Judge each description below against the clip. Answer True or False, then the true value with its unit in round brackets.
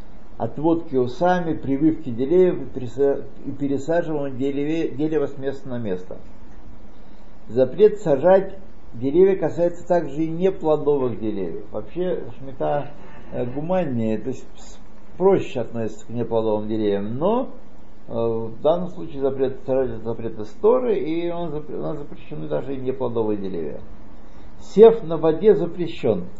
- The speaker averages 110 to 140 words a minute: True (115 wpm)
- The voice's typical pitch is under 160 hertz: True (140 Hz)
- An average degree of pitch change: False (5.8 semitones)